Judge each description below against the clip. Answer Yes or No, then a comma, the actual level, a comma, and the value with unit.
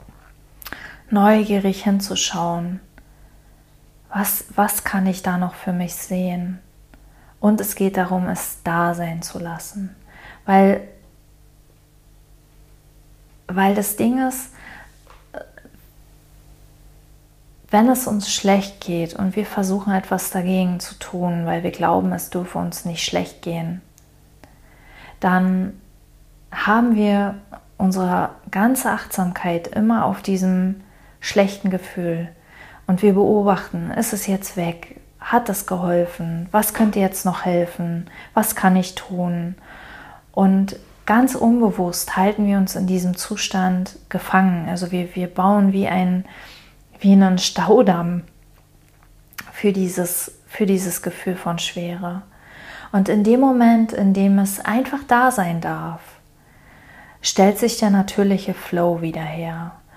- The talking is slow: Yes, slow, 120 wpm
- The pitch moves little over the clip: Yes, narrow, 2.3 semitones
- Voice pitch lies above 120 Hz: Yes, high, 190 Hz